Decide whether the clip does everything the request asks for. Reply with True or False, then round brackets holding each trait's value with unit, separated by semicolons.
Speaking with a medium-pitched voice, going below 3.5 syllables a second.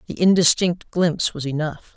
False (165 Hz; 5.1 syllables/s)